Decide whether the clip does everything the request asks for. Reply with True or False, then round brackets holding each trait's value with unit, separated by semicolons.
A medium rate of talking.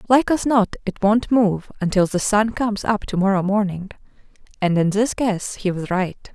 True (190 wpm)